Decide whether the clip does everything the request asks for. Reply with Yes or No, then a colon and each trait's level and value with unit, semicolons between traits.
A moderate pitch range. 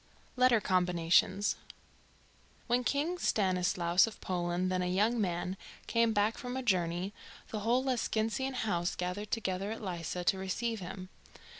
Yes: average, 4.2 semitones